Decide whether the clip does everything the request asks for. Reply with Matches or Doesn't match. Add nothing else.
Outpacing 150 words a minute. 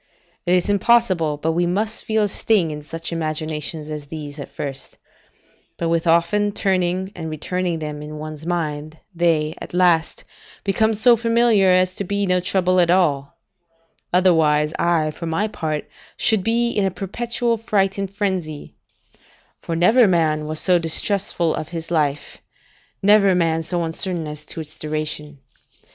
Matches